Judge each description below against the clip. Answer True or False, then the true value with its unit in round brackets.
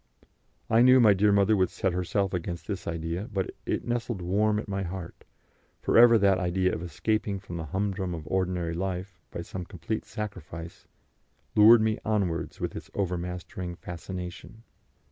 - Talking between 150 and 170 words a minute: True (165 wpm)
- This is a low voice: True (95 Hz)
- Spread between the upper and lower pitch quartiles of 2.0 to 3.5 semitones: True (3.1 semitones)